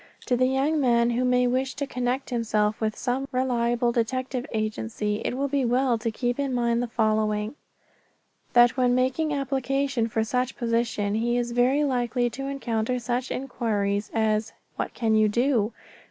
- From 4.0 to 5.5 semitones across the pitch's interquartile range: No, narrow, 2.5 semitones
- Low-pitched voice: No, high, 245 Hz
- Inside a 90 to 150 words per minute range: No, average, 165 wpm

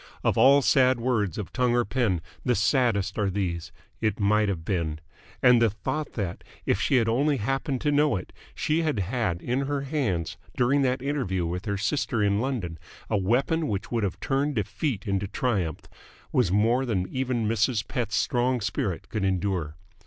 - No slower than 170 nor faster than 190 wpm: Yes, average, 180 wpm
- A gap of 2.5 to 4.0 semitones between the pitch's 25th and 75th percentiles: No, average, 4.9 semitones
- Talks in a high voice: No, low, 115 Hz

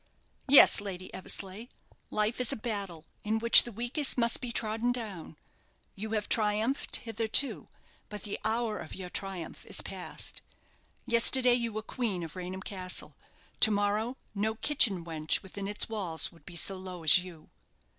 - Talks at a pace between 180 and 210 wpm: No, average, 160 wpm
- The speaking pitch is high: Yes, high, 210 Hz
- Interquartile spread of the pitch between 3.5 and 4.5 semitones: Yes, average, 3.8 semitones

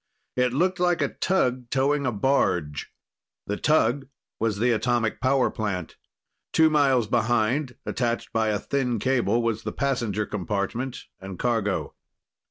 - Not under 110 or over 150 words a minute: Yes, average, 140 wpm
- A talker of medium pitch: No, low, 120 Hz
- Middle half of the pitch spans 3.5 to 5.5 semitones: Yes, average, 3.8 semitones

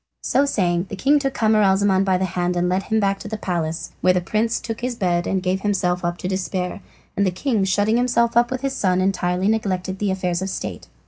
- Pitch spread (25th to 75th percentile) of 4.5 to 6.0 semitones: No, average, 3.3 semitones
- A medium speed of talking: No, fast, 240 wpm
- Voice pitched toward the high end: Yes, high, 195 Hz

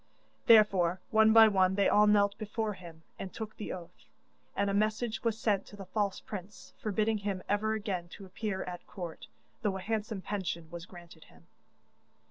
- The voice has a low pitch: No, high, 200 Hz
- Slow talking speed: No, average, 180 wpm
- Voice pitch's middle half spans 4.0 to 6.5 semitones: No, average, 2.7 semitones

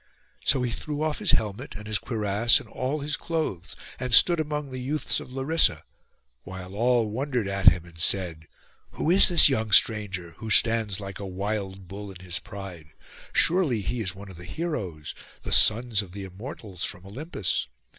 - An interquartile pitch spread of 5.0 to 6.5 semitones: Yes, wide, 5.6 semitones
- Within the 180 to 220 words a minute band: Yes, average, 185 wpm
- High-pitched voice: No, low, 105 Hz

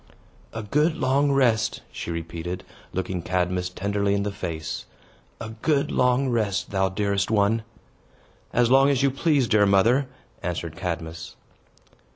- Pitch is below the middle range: Yes, low, 100 Hz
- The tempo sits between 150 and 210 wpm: No, average, 140 wpm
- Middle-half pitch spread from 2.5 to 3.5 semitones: No, wide, 5.6 semitones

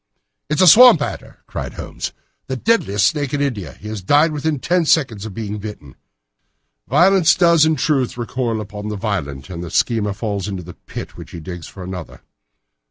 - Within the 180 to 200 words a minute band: Yes, average, 190 wpm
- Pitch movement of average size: No, wide, 7.5 semitones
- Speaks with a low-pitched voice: Yes, low, 110 Hz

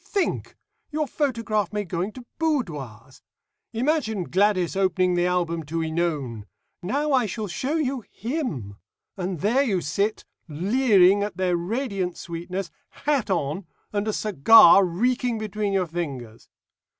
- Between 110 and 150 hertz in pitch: No, high, 195 Hz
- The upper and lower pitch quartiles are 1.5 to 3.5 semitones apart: No, average, 5.3 semitones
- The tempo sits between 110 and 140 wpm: Yes, slow, 135 wpm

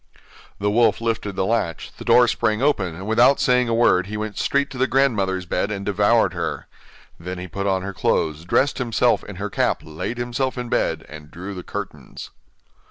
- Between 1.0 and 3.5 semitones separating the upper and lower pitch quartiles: No, average, 4.6 semitones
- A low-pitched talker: Yes, low, 105 Hz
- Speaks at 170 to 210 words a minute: Yes, average, 200 wpm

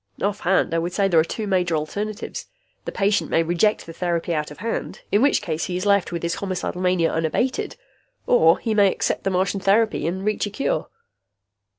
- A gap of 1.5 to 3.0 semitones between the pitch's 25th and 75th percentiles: No, average, 3.4 semitones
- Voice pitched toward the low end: No, medium, 185 Hz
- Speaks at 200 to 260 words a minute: Yes, fast, 205 wpm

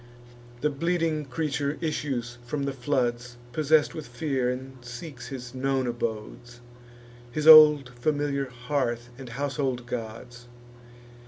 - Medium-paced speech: No, slow, 115 wpm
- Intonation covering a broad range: No, average, 3.3 semitones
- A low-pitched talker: Yes, low, 130 Hz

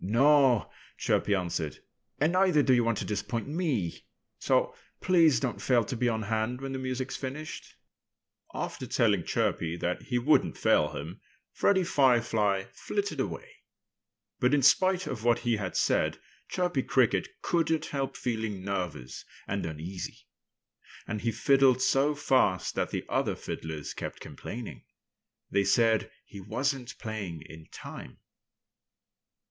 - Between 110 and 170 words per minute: Yes, average, 140 wpm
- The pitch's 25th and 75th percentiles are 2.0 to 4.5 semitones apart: No, average, 5.2 semitones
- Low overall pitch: Yes, low, 120 Hz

